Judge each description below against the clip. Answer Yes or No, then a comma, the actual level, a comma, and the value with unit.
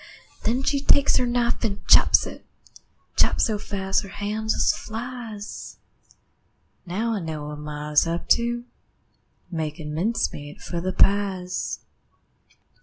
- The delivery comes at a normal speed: No, slow, 130 wpm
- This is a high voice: Yes, high, 200 Hz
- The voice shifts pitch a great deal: Yes, wide, 5.8 semitones